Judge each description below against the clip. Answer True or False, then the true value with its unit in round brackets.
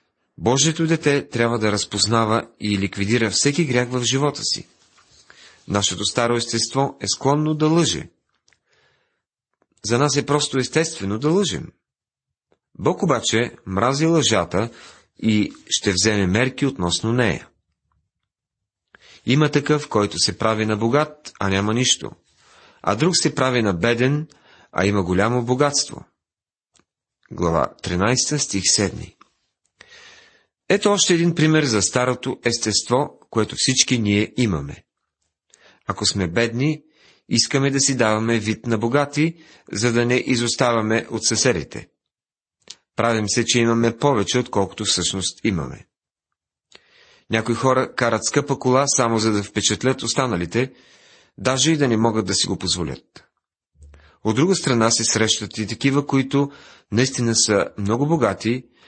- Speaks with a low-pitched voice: True (120 Hz)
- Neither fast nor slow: True (130 wpm)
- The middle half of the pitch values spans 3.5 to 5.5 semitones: True (5.1 semitones)